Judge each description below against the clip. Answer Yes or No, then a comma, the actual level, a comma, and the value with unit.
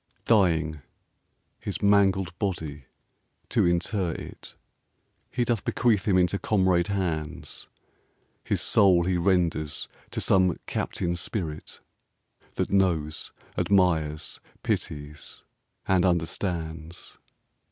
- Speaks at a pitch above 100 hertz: No, very low, 90 Hz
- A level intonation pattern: No, average, 3.3 semitones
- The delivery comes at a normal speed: No, slow, 95 wpm